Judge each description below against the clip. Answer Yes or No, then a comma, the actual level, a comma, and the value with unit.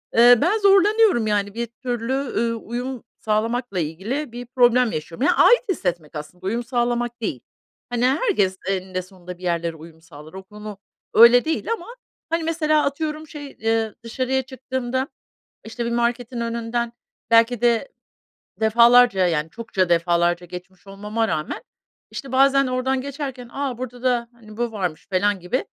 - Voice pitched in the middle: No, high, 235 Hz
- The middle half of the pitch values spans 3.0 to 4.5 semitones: No, average, 5.1 semitones